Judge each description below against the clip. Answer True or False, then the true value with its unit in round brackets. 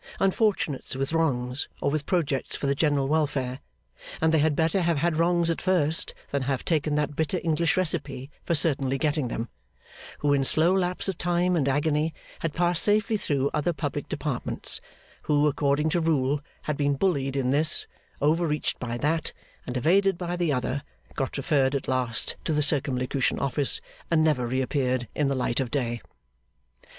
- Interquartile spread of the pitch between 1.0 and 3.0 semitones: False (3.4 semitones)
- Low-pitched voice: False (150 Hz)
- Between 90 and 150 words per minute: False (175 wpm)